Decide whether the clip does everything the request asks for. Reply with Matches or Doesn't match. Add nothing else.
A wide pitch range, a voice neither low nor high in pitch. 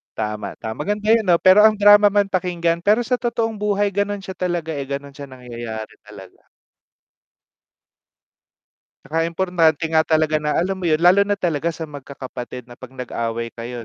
Matches